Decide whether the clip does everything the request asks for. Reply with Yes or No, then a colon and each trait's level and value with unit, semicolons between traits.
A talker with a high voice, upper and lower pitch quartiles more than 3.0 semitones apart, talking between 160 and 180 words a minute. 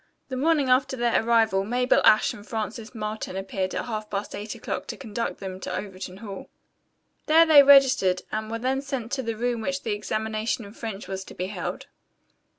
No: high, 220 Hz; average, 3.6 semitones; average, 195 wpm